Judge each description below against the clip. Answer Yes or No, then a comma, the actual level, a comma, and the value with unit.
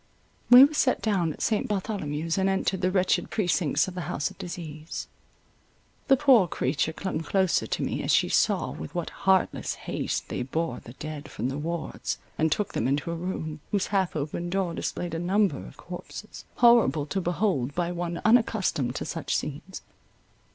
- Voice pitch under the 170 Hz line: No, medium, 175 Hz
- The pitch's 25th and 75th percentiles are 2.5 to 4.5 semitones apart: Yes, average, 4.0 semitones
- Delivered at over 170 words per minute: Yes, average, 180 wpm